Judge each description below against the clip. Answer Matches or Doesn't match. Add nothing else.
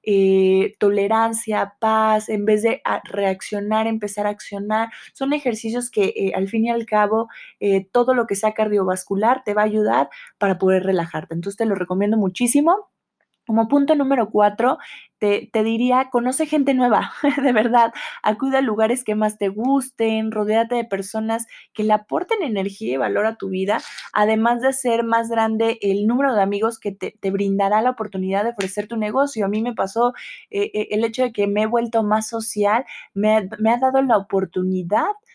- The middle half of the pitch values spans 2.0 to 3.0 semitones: Matches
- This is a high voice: Matches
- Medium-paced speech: Matches